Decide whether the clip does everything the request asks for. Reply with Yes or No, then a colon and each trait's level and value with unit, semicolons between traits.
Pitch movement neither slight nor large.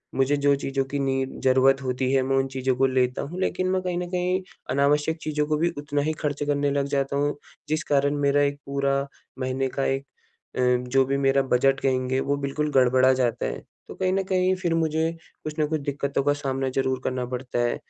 No: narrow, 2.1 semitones